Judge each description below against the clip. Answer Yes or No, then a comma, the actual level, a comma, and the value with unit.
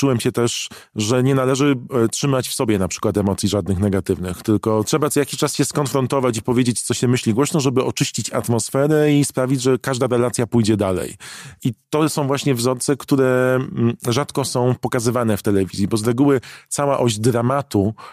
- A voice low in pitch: Yes, low, 125 Hz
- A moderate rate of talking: No, fast, 180 wpm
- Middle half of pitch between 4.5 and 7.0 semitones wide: No, average, 3.6 semitones